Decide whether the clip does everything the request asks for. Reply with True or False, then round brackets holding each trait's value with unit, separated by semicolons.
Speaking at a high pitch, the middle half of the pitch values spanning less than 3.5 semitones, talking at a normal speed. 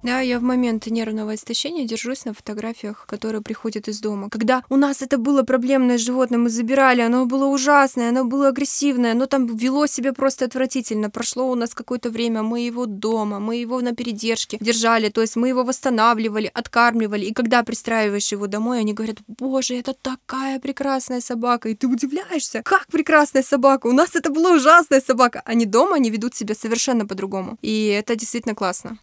False (245 Hz; 3.0 semitones; 180 wpm)